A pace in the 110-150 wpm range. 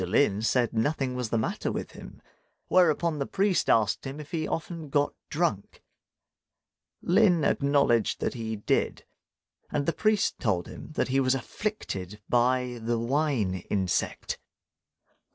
Yes: average, 140 wpm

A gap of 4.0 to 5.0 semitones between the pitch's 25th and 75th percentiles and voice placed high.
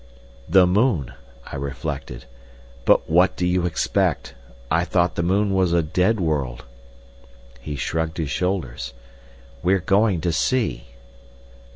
No: average, 4.5 semitones; very low, 85 Hz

